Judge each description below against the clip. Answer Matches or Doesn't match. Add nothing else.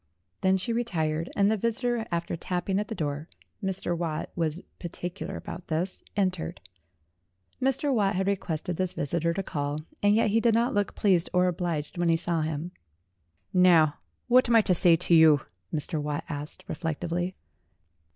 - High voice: Doesn't match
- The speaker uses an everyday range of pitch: Matches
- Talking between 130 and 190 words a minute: Matches